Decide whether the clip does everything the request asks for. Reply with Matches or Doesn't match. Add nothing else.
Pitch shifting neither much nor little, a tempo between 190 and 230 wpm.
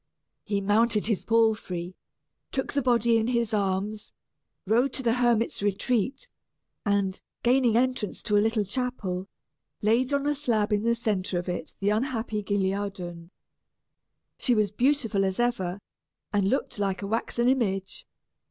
Doesn't match